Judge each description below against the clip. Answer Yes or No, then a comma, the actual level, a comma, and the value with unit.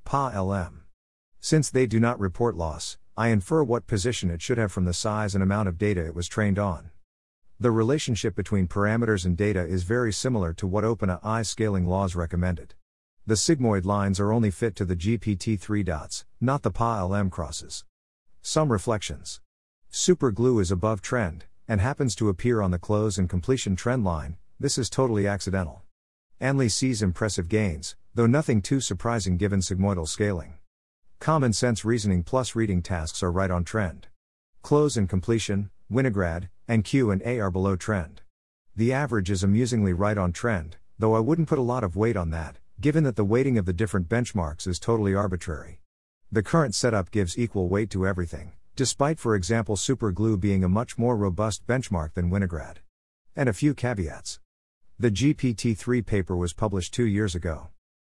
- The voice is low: Yes, low, 100 Hz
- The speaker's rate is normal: Yes, average, 175 wpm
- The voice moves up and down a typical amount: Yes, average, 4.4 semitones